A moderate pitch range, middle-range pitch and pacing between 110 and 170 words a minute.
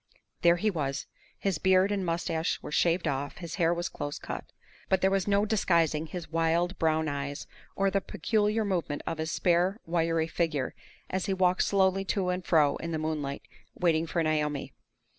No: average, 3.1 semitones; medium, 170 Hz; average, 180 wpm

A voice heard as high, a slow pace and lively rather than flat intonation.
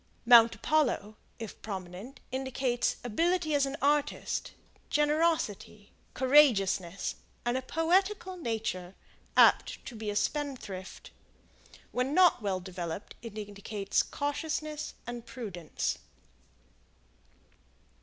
Yes: high, 240 Hz; slow, 95 wpm; wide, 6.4 semitones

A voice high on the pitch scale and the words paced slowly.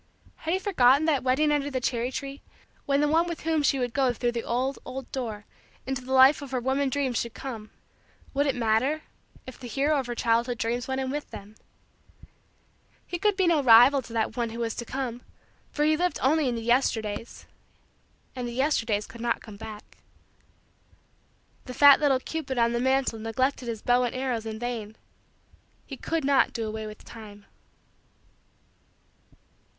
No: very high, 255 Hz; average, 185 wpm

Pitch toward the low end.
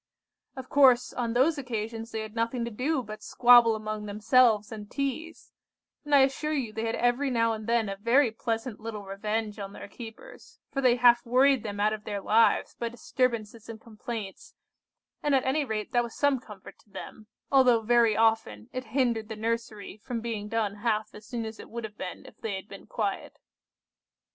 No: high, 230 Hz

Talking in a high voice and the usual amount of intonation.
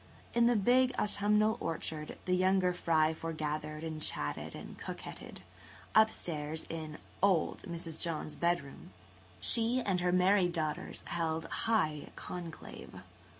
No: medium, 170 Hz; average, 4.2 semitones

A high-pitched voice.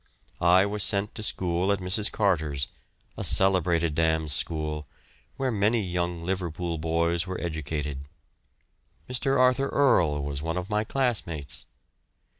No: very low, 90 Hz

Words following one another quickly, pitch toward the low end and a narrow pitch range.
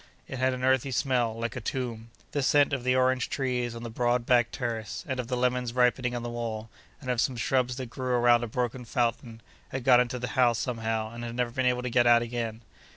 Yes: fast, 240 wpm; low, 125 Hz; narrow, 1.5 semitones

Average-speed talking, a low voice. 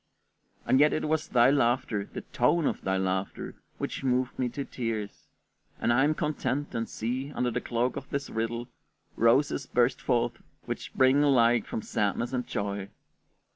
Yes: average, 170 wpm; low, 125 Hz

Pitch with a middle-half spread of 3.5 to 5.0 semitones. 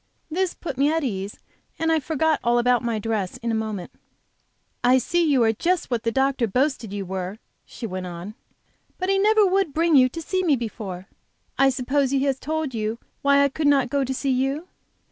No: wide, 5.5 semitones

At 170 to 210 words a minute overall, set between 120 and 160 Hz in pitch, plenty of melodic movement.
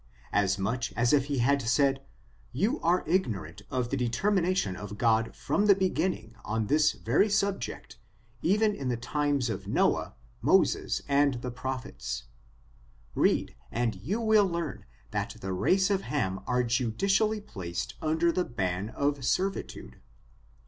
No: average, 145 wpm; low, 135 Hz; wide, 8.4 semitones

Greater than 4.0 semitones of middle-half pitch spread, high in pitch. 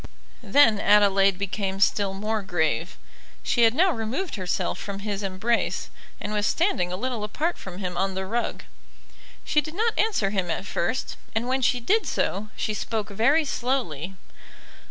Yes: average, 4.6 semitones; high, 210 Hz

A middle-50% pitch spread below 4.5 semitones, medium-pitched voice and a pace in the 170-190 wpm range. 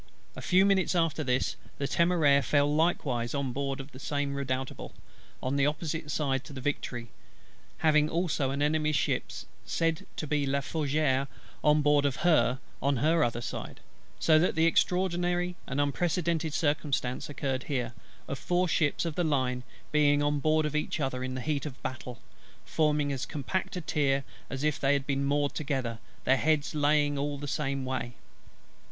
Yes: narrow, 2.5 semitones; medium, 145 Hz; average, 175 wpm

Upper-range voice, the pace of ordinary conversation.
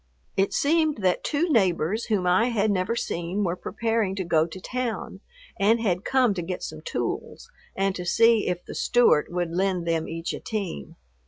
Yes: high, 195 Hz; average, 185 wpm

